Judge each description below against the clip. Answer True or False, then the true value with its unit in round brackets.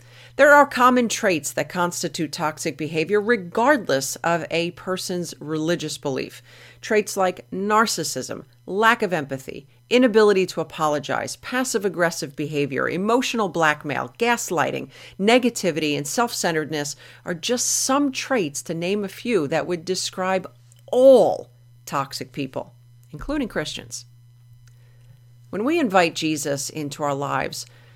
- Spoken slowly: True (120 wpm)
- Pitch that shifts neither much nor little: False (7.2 semitones)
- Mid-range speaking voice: True (165 Hz)